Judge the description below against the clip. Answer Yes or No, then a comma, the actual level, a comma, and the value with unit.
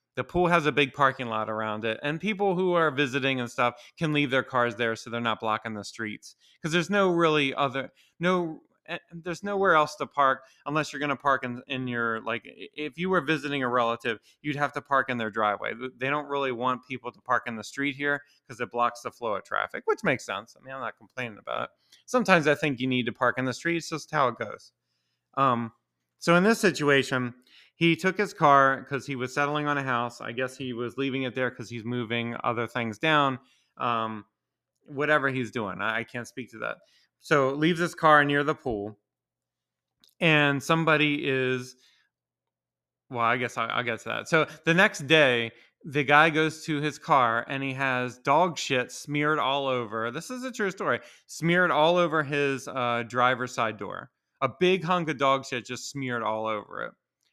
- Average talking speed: No, fast, 210 wpm